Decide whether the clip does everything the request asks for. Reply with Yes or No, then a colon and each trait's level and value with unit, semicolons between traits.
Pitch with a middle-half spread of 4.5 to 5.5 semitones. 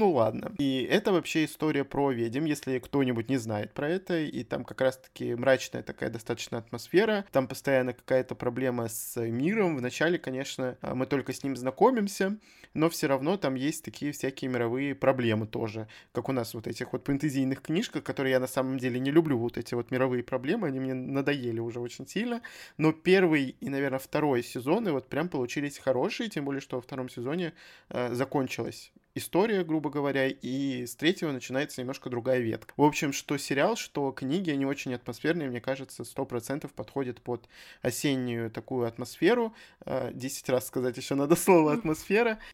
No: average, 3.3 semitones